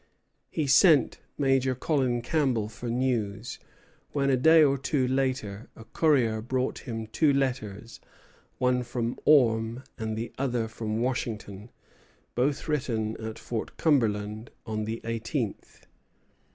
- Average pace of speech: No, slow, 125 wpm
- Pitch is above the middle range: No, low, 120 Hz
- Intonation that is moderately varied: Yes, average, 3.3 semitones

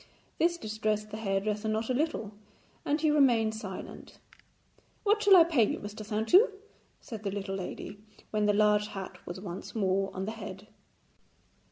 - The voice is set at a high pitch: Yes, high, 215 Hz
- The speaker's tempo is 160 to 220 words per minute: Yes, average, 165 wpm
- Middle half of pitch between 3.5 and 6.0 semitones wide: No, average, 2.8 semitones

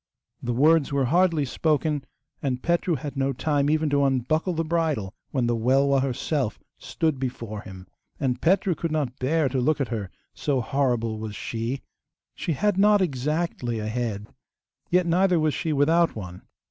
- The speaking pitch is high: No, medium, 140 Hz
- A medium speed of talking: Yes, average, 170 wpm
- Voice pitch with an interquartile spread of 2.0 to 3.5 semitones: No, average, 4.8 semitones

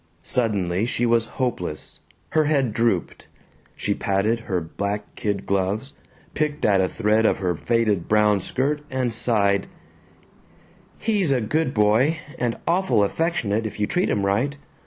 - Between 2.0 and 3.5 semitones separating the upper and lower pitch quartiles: No, average, 4.6 semitones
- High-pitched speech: No, low, 110 Hz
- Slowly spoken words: No, average, 145 wpm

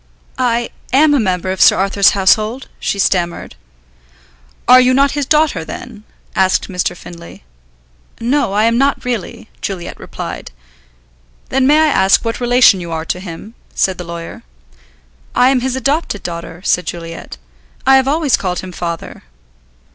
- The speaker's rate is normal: Yes, average, 155 wpm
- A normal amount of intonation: No, wide, 6.3 semitones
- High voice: Yes, high, 215 Hz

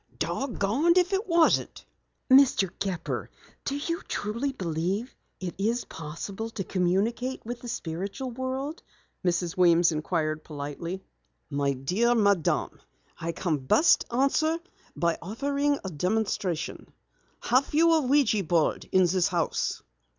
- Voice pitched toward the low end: No, high, 200 Hz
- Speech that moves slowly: Yes, slow, 125 wpm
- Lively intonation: Yes, wide, 7.5 semitones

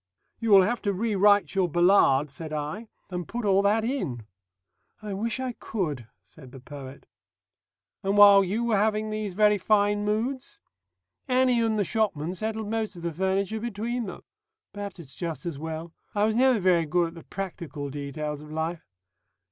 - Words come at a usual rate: Yes, average, 175 wpm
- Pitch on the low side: No, high, 195 Hz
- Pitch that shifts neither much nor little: Yes, average, 4.9 semitones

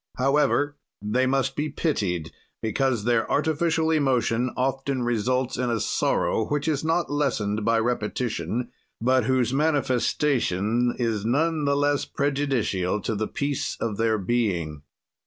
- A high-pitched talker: No, low, 125 Hz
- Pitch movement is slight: No, average, 4.3 semitones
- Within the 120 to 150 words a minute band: Yes, slow, 135 wpm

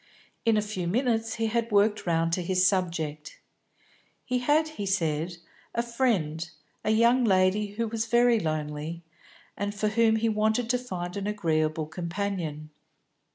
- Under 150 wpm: No, average, 155 wpm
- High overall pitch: Yes, high, 205 Hz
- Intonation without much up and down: No, average, 5.1 semitones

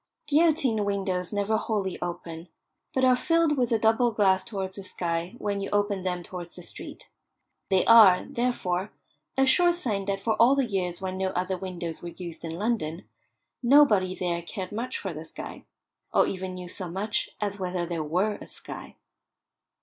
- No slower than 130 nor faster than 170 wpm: No, average, 180 wpm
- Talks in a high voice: Yes, high, 195 Hz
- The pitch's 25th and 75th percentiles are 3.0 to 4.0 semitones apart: Yes, average, 3.7 semitones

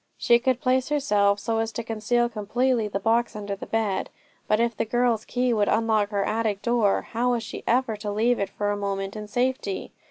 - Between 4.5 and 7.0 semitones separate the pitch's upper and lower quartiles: No, average, 2.7 semitones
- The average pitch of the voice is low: No, high, 225 Hz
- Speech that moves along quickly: Yes, fast, 215 wpm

